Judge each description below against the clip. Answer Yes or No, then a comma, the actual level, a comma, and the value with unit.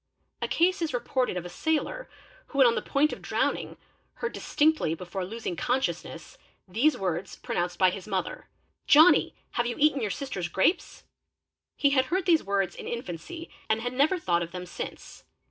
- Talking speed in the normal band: Yes, average, 180 wpm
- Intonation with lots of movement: Yes, wide, 8.7 semitones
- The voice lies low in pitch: No, high, 240 Hz